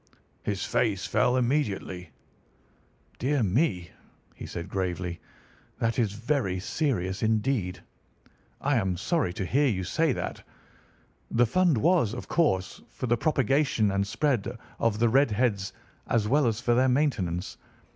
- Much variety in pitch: Yes, wide, 5.8 semitones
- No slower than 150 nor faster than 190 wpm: No, average, 140 wpm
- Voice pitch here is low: Yes, low, 115 Hz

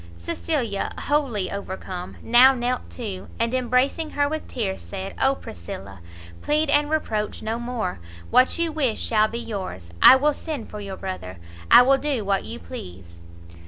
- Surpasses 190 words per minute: No, average, 160 wpm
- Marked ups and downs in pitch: Yes, wide, 6.1 semitones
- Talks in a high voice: Yes, high, 230 Hz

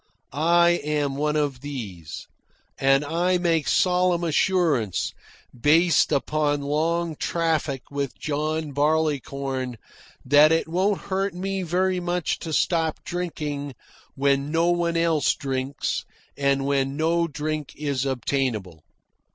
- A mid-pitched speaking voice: Yes, medium, 150 Hz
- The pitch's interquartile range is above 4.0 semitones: No, average, 3.5 semitones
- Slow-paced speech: Yes, slow, 120 wpm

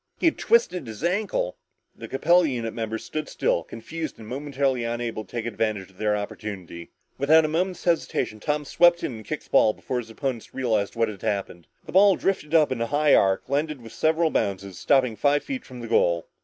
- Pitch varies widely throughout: Yes, wide, 6.2 semitones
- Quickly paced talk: Yes, fast, 210 wpm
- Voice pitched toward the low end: Yes, low, 125 Hz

